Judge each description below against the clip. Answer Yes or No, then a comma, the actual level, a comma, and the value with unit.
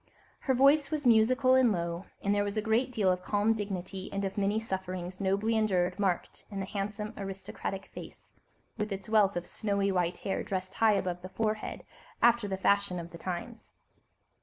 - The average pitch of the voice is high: Yes, high, 200 Hz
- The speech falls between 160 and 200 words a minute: Yes, average, 185 wpm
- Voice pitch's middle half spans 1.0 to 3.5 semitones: Yes, average, 2.8 semitones